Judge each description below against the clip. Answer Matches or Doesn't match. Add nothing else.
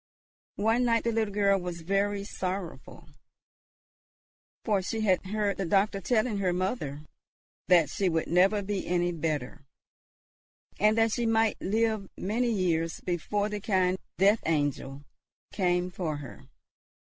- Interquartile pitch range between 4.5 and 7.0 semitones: Doesn't match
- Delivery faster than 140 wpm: Doesn't match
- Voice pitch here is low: Doesn't match